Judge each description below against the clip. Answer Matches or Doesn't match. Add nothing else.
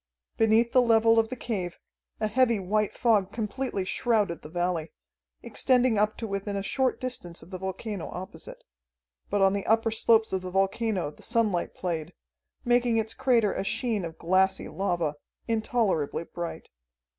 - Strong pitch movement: Doesn't match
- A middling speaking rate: Matches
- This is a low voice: Doesn't match